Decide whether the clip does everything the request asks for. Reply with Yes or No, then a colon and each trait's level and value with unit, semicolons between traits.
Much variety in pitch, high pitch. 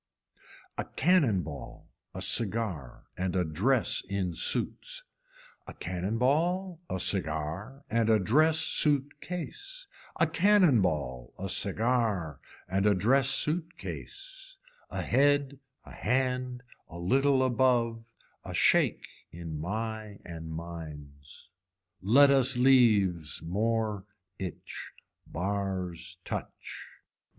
No: wide, 7.4 semitones; low, 110 Hz